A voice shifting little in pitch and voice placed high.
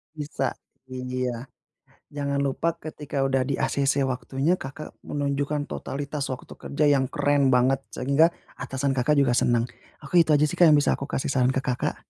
No: narrow, 1.9 semitones; medium, 140 Hz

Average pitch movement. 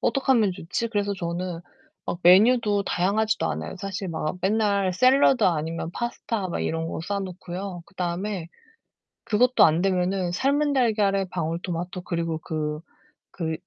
Yes: average, 3.6 semitones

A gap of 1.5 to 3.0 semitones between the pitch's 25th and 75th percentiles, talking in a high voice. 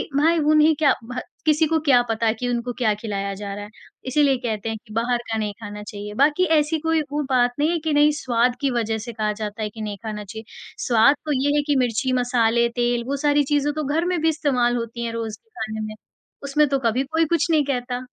No: average, 4.9 semitones; high, 245 Hz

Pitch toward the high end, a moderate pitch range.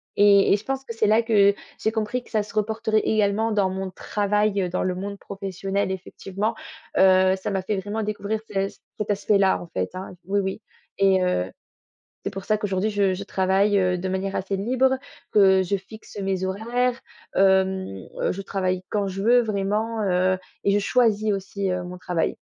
No: high, 200 Hz; narrow, 2.0 semitones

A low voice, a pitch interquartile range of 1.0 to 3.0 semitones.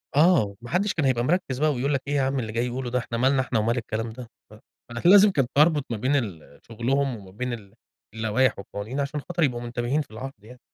No: low, 125 Hz; average, 3.5 semitones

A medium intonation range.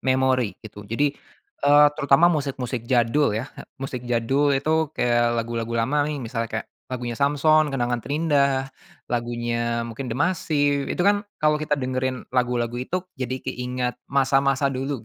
Yes: average, 3.2 semitones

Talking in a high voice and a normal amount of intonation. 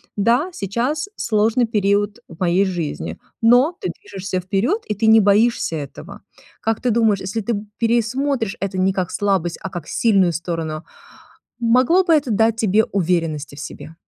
Yes: high, 205 Hz; average, 4.1 semitones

